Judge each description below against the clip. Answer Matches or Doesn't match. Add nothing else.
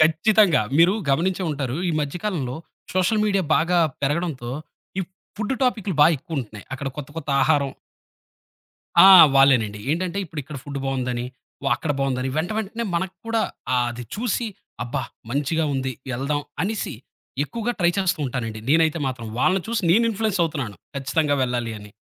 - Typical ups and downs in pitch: Doesn't match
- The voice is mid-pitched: Matches